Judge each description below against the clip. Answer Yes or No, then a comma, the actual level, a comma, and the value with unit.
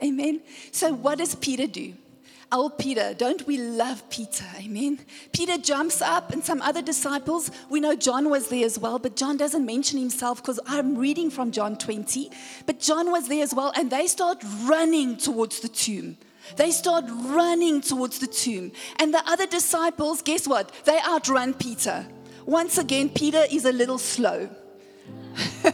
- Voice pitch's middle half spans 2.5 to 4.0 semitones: Yes, average, 3.7 semitones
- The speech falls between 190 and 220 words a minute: No, average, 170 wpm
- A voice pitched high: Yes, very high, 285 Hz